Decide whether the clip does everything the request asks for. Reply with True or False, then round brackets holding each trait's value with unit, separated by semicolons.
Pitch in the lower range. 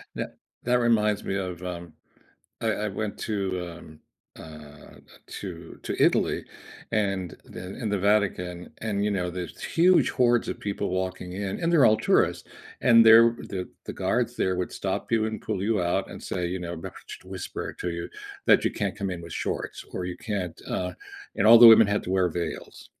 True (95 Hz)